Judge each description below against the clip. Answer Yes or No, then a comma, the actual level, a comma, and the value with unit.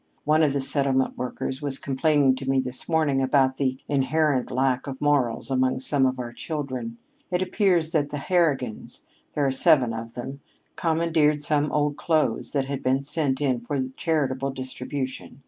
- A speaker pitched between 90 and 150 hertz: Yes, low, 135 Hz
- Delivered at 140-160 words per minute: No, average, 170 wpm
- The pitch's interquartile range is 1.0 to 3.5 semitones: Yes, narrow, 2.4 semitones